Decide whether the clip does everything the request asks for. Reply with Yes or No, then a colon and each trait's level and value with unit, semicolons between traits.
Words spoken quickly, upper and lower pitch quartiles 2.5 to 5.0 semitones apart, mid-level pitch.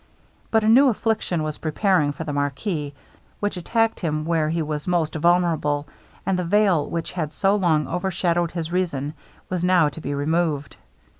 No: average, 170 wpm; average, 3.3 semitones; medium, 170 Hz